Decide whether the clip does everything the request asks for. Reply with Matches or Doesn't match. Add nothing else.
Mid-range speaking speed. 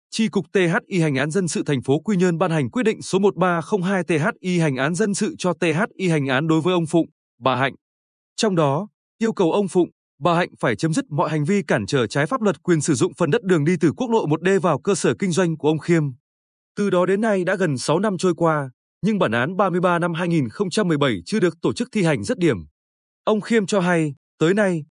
Matches